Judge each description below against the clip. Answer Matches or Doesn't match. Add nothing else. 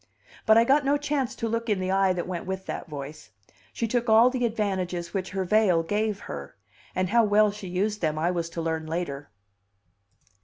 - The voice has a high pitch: Matches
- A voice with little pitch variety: Doesn't match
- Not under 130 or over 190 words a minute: Doesn't match